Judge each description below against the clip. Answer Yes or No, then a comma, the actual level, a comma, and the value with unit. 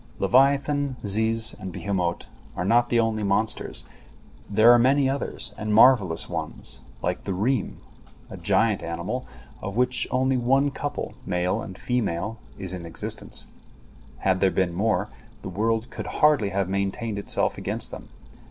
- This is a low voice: Yes, low, 110 Hz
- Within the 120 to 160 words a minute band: Yes, average, 150 wpm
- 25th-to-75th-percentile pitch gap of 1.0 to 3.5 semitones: No, average, 4.7 semitones